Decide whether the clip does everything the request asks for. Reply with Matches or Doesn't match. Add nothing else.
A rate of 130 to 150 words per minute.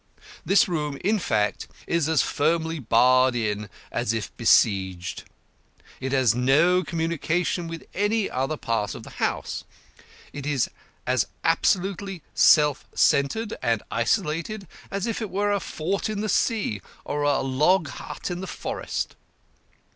Matches